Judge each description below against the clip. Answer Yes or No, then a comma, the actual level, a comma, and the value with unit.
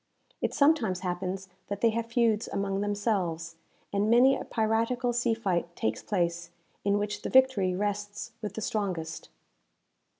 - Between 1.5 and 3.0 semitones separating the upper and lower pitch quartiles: No, average, 3.8 semitones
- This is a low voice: No, high, 205 Hz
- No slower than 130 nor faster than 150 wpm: Yes, average, 145 wpm